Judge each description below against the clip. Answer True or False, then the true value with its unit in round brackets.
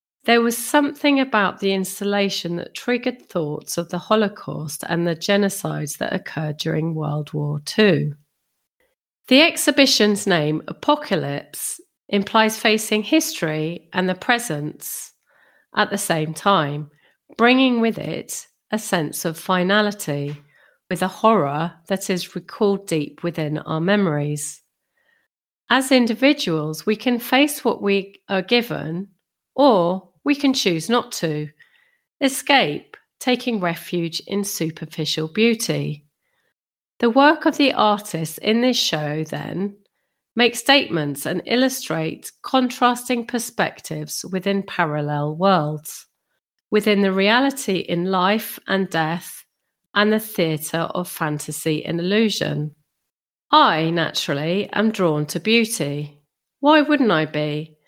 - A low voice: False (195 Hz)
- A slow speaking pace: True (120 wpm)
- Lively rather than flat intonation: True (7.0 semitones)